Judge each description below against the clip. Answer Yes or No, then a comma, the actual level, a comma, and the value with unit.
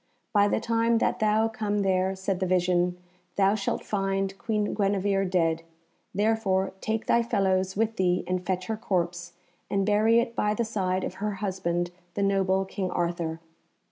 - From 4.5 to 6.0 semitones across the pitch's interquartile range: No, narrow, 2.5 semitones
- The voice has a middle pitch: No, high, 195 Hz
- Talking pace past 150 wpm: Yes, average, 170 wpm